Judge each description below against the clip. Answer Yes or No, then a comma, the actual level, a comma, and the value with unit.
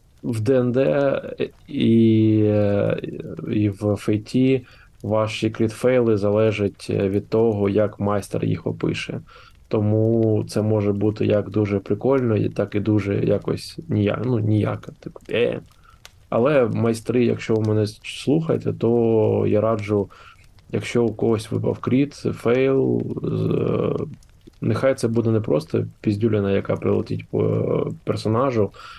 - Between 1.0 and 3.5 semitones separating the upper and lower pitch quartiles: Yes, narrow, 2.6 semitones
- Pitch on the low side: Yes, low, 110 Hz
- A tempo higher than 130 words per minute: No, average, 125 wpm